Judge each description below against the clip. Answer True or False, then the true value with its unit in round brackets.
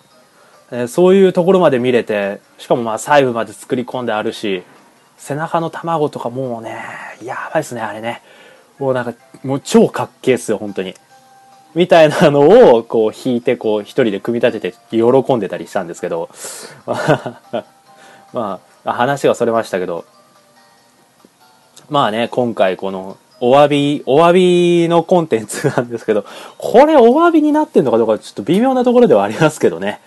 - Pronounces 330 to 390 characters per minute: True (335 characters per minute)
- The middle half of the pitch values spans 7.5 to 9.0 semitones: False (6.9 semitones)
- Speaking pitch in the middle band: False (130 Hz)